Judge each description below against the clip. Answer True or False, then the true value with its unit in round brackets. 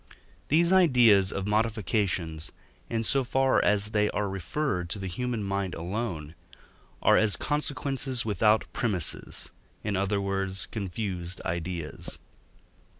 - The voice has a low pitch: True (105 Hz)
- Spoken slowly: True (120 wpm)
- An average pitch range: True (3.9 semitones)